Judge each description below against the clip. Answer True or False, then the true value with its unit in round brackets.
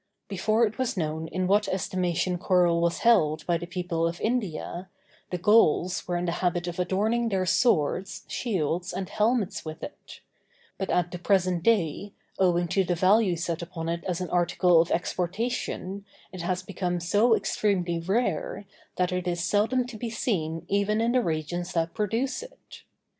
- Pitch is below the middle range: False (180 Hz)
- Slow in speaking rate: False (175 wpm)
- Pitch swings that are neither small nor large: True (3.3 semitones)